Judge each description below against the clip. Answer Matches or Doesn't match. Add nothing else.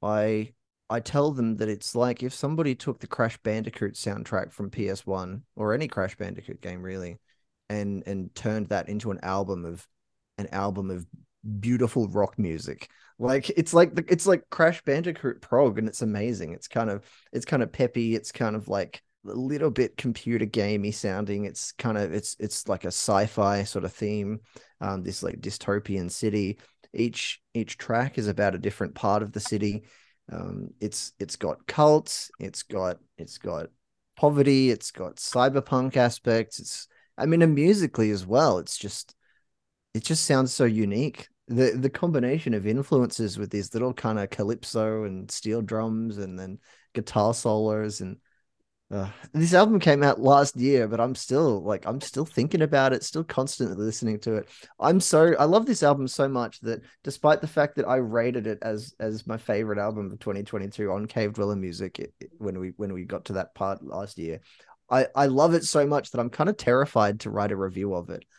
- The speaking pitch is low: Matches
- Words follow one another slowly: Doesn't match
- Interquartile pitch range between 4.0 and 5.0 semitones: Matches